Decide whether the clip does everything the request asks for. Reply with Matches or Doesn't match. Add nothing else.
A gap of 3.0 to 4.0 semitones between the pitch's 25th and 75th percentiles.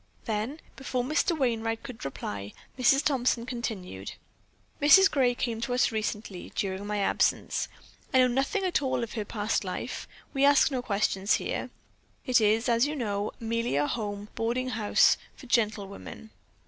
Matches